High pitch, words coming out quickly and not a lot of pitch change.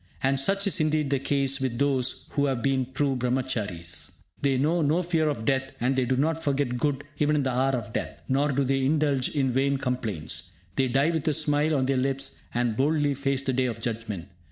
No: low, 135 Hz; fast, 220 wpm; narrow, 2.3 semitones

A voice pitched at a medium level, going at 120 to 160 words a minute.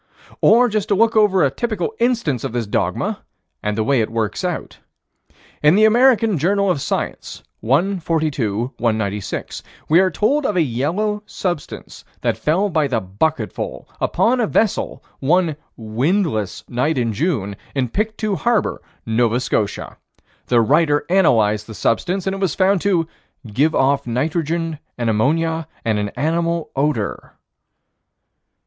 Yes: medium, 155 Hz; average, 145 wpm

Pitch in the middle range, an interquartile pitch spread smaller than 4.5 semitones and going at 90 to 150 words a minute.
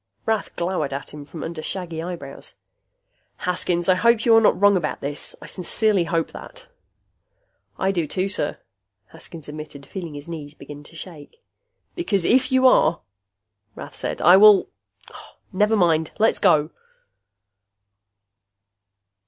No: medium, 175 Hz; average, 4.9 semitones; average, 140 wpm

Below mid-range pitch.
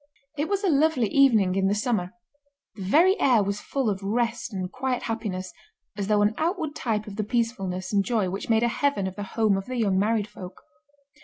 No: high, 215 Hz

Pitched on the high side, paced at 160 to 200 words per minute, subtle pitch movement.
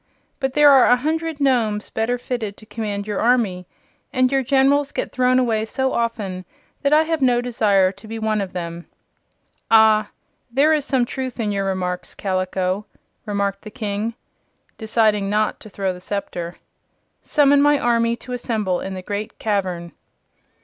No: high, 220 Hz; average, 165 wpm; average, 4.4 semitones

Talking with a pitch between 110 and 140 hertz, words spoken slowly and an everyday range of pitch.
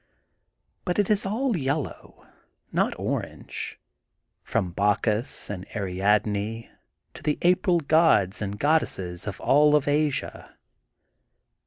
No: low, 135 Hz; slow, 115 wpm; wide, 7.9 semitones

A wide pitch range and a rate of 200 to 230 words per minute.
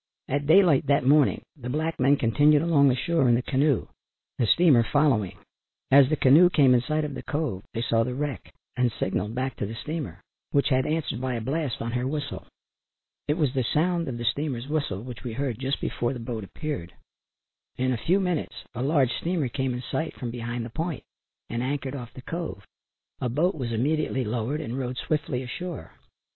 No: average, 4.0 semitones; fast, 205 wpm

